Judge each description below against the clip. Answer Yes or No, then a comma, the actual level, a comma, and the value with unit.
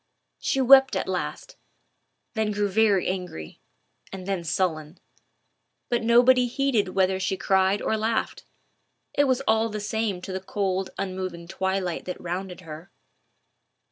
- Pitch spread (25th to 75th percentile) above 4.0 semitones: No, average, 3.3 semitones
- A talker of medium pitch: No, high, 195 Hz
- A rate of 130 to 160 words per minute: Yes, average, 140 wpm